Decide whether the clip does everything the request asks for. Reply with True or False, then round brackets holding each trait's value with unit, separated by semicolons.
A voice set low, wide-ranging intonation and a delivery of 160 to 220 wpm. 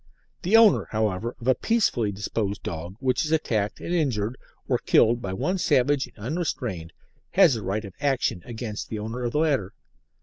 True (120 Hz; 5.9 semitones; 180 wpm)